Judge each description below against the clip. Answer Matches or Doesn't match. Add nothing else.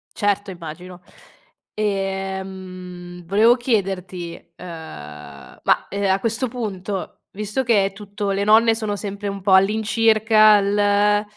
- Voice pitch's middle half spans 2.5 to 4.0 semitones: Doesn't match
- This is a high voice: Matches